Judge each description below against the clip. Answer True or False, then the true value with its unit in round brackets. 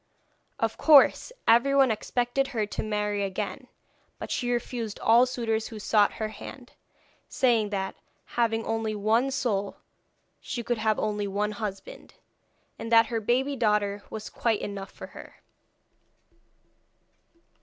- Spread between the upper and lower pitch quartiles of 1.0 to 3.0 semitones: True (2.6 semitones)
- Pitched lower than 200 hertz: False (225 Hz)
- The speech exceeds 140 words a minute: False (135 wpm)